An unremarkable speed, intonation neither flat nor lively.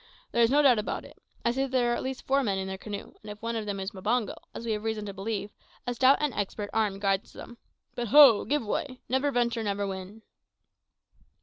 No: fast, 240 wpm; average, 3.5 semitones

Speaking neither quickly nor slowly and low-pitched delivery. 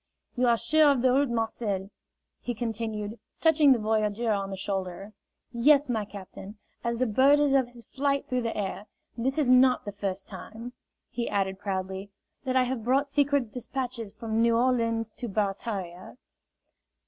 No: average, 170 wpm; high, 230 Hz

